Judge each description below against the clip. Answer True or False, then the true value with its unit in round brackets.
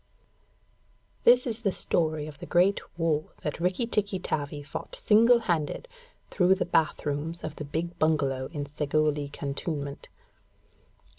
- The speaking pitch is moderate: True (160 Hz)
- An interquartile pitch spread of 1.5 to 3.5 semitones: False (4.4 semitones)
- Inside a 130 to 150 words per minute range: True (145 wpm)